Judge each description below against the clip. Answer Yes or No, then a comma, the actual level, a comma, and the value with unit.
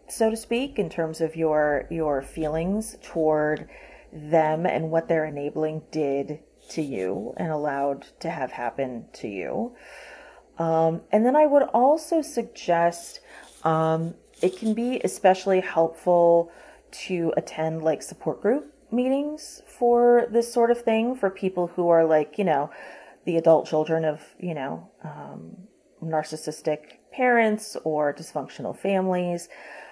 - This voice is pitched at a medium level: Yes, medium, 165 Hz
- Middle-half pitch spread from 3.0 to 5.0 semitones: No, wide, 5.4 semitones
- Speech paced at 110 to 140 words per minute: Yes, slow, 135 wpm